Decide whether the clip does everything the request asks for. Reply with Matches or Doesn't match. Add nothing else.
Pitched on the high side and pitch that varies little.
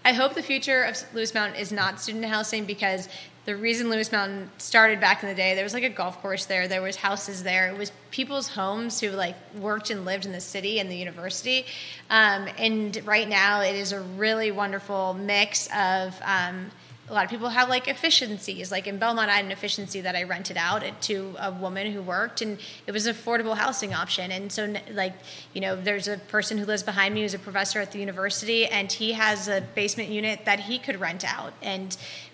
Matches